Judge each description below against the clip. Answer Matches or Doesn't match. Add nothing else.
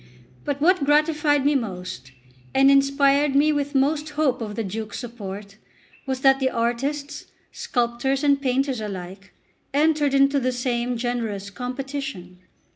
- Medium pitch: Doesn't match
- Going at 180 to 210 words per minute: Doesn't match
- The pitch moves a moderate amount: Matches